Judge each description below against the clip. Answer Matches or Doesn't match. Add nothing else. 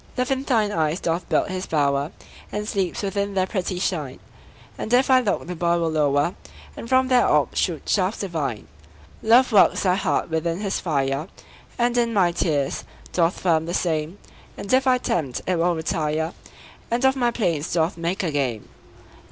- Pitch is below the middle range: Doesn't match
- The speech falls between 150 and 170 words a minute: Doesn't match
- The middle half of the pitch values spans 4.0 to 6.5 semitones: Matches